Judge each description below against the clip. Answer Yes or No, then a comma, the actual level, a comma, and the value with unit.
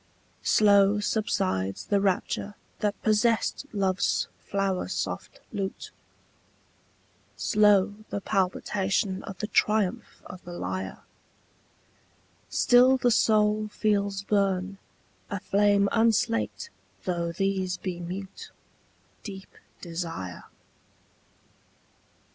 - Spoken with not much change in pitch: Yes, narrow, 2.1 semitones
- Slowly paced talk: Yes, slow, 90 wpm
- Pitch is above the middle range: Yes, high, 200 Hz